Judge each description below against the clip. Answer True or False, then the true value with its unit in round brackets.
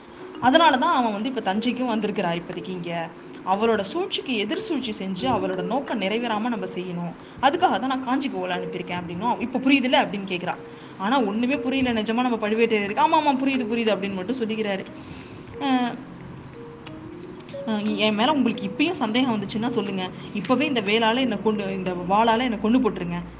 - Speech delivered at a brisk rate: True (155 wpm)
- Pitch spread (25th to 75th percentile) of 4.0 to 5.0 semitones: True (4.4 semitones)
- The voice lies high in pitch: True (225 Hz)